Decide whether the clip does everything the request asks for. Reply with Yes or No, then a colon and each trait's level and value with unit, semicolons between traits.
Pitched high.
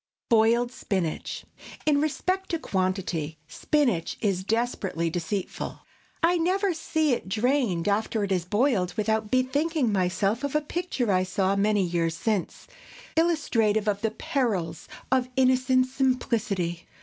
Yes: high, 220 Hz